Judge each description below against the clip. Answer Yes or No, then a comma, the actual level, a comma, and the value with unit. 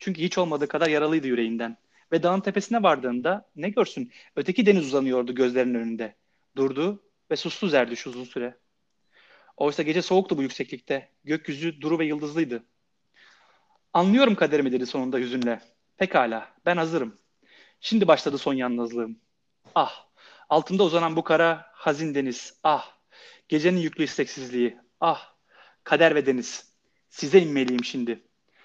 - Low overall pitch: No, medium, 150 Hz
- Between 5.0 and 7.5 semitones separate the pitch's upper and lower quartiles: Yes, average, 5.3 semitones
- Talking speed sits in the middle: Yes, average, 130 wpm